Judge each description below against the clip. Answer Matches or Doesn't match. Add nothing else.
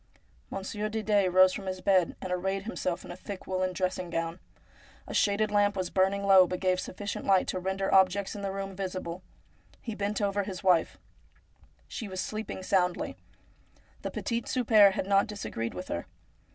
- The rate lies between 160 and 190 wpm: Matches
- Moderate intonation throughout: Doesn't match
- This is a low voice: Doesn't match